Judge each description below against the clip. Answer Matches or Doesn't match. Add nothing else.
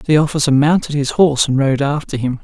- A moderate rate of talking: Doesn't match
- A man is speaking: Matches